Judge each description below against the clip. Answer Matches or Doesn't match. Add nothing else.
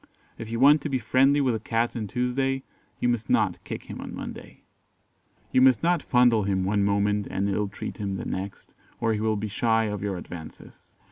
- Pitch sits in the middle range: Doesn't match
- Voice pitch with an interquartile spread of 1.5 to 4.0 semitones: Matches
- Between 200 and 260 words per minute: Matches